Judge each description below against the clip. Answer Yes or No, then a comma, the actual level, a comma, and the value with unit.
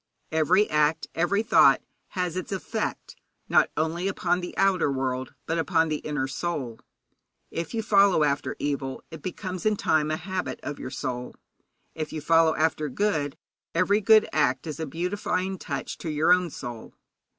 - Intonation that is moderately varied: Yes, average, 3.8 semitones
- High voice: No, medium, 165 Hz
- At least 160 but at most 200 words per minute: Yes, average, 165 wpm